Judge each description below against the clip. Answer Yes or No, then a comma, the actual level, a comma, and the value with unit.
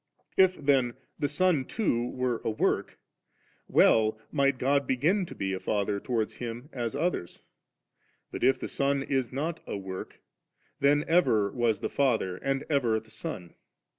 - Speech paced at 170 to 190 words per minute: No, average, 160 wpm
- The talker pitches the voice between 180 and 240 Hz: No, low, 130 Hz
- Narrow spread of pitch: No, average, 4.4 semitones